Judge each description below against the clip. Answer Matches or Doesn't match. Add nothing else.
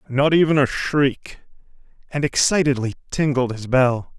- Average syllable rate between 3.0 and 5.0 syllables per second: Matches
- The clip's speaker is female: Doesn't match